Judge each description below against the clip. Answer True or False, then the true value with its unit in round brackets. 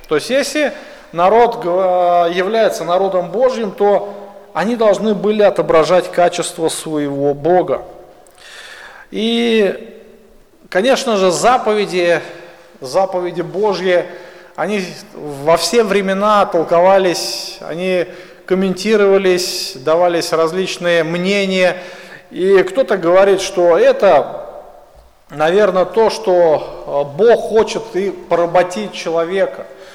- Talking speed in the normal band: False (90 wpm)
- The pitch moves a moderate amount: True (3.0 semitones)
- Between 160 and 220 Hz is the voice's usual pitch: True (185 Hz)